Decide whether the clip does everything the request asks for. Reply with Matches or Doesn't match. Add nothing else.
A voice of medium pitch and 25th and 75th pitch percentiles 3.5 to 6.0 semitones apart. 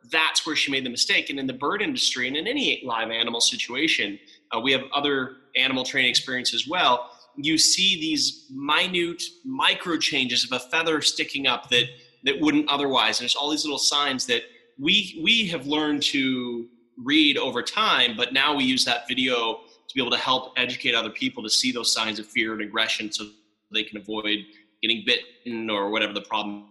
Doesn't match